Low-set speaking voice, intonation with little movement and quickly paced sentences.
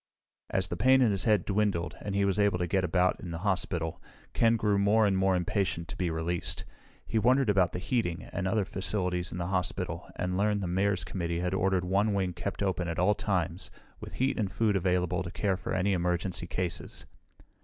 Yes: very low, 95 Hz; narrow, 2.3 semitones; fast, 210 wpm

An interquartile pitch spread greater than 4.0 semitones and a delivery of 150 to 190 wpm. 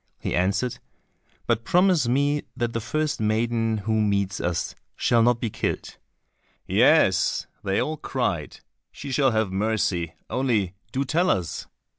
No: average, 4.9 semitones; average, 140 wpm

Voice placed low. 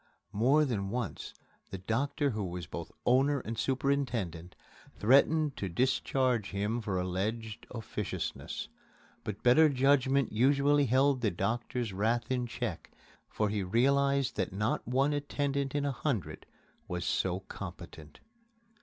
Yes: low, 120 Hz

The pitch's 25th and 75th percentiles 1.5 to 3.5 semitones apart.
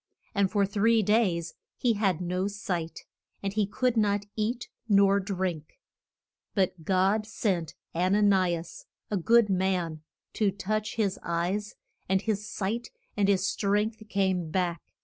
Yes: narrow, 2.5 semitones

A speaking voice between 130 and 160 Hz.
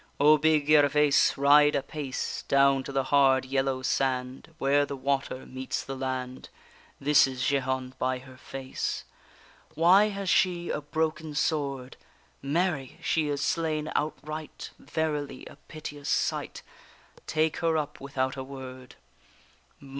Yes: medium, 140 Hz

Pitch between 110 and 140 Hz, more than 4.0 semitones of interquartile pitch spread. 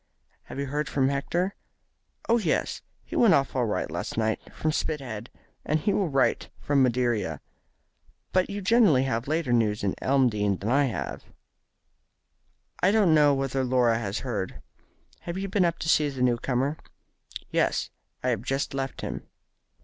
Yes: low, 135 Hz; average, 4.7 semitones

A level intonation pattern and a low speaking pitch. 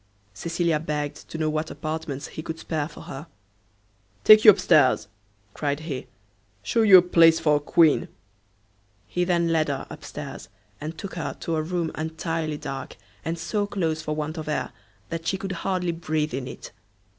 No: narrow, 2.0 semitones; medium, 160 Hz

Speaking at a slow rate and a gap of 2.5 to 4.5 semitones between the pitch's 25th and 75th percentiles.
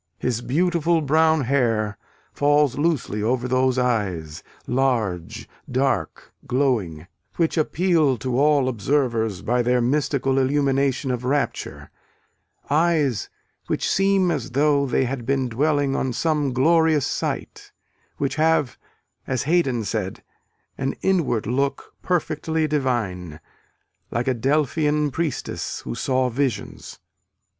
Yes: slow, 115 wpm; average, 3.7 semitones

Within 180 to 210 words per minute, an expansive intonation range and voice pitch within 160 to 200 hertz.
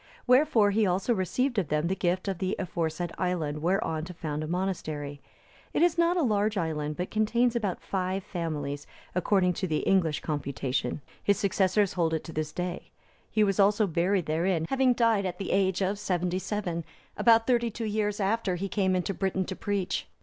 No: average, 190 wpm; average, 3.7 semitones; high, 190 Hz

